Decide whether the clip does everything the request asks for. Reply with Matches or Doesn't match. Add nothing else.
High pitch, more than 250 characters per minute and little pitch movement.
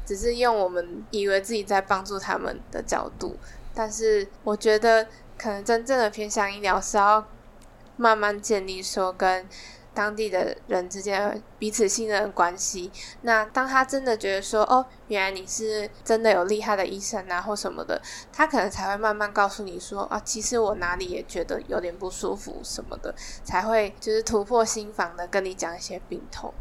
Matches